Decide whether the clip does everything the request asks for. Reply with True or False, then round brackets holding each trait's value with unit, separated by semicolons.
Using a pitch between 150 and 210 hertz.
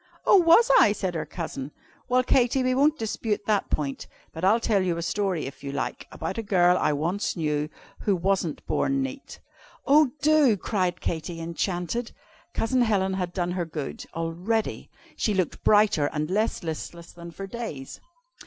True (190 Hz)